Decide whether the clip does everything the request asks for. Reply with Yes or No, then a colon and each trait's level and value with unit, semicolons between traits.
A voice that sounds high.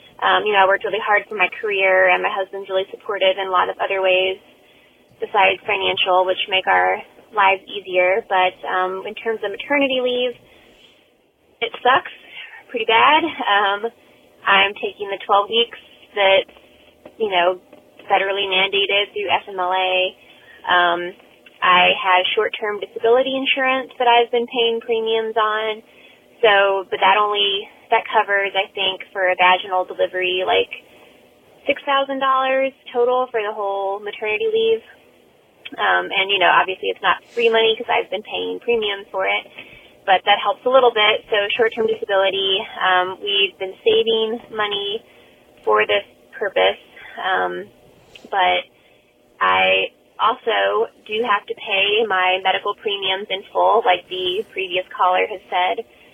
Yes: high, 205 Hz